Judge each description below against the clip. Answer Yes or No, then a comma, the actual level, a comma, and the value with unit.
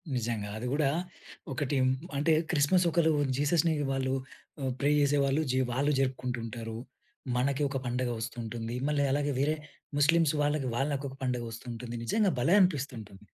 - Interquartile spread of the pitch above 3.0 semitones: Yes, average, 3.5 semitones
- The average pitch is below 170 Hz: Yes, low, 135 Hz